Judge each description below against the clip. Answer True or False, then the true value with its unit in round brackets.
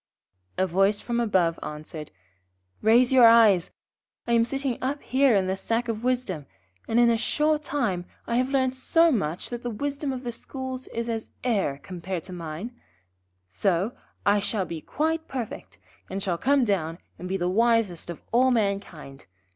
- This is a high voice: True (225 Hz)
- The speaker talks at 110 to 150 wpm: False (175 wpm)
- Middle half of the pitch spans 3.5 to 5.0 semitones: False (5.6 semitones)